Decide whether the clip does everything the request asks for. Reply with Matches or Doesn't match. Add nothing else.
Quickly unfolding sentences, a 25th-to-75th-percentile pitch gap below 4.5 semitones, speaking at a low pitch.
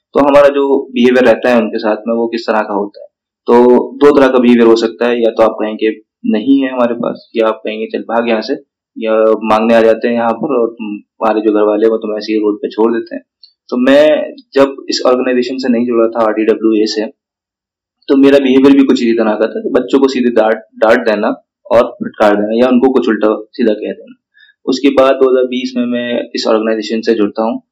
Matches